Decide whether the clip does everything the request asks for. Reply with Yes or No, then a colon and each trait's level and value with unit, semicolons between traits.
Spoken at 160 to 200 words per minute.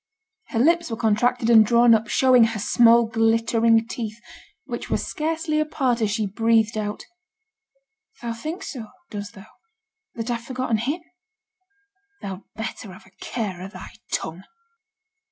No: average, 145 wpm